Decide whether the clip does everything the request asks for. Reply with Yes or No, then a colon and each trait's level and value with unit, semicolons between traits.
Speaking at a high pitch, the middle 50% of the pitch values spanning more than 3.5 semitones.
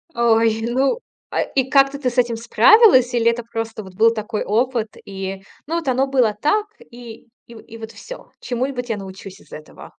No: high, 235 Hz; average, 2.9 semitones